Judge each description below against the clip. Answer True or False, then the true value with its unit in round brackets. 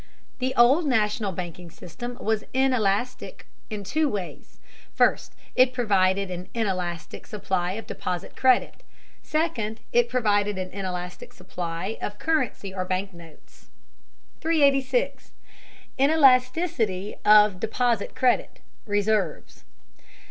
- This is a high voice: True (210 Hz)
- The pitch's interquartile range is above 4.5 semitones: True (5.3 semitones)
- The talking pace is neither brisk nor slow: False (105 wpm)